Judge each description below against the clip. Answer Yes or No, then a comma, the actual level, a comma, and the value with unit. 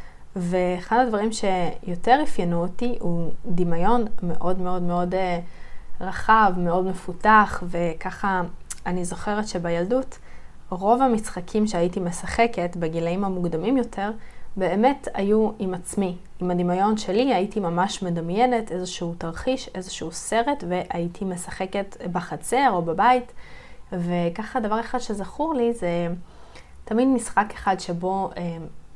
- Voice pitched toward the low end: No, medium, 185 Hz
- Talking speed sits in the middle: Yes, average, 110 wpm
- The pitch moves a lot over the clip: No, average, 3.7 semitones